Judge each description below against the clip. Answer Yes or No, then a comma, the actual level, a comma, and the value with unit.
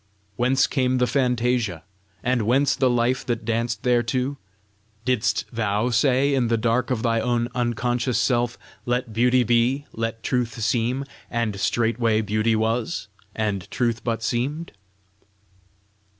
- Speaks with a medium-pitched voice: No, low, 120 Hz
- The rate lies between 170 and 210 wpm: No, slow, 135 wpm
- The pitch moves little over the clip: Yes, narrow, 1.8 semitones